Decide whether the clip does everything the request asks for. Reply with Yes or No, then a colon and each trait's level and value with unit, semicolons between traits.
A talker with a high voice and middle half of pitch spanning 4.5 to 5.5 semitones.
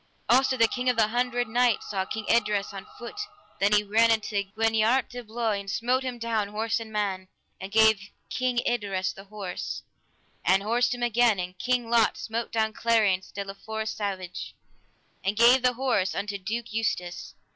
No: high, 220 Hz; average, 3.0 semitones